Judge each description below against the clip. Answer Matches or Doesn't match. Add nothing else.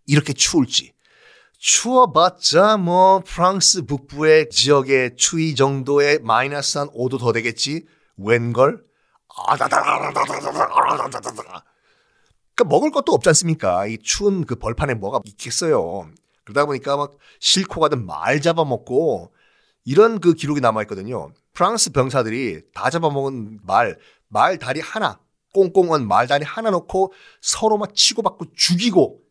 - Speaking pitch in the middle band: Matches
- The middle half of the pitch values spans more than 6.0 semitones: Doesn't match